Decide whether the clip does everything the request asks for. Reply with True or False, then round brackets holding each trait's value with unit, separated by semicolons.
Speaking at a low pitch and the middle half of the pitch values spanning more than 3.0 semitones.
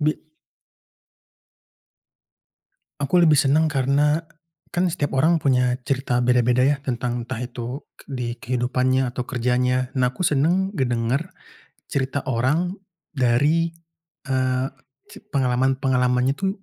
False (130 Hz; 2.7 semitones)